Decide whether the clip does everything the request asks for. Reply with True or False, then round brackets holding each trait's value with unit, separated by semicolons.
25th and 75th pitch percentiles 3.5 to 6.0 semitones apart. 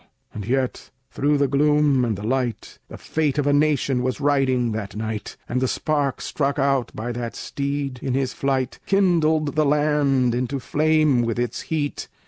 False (3.1 semitones)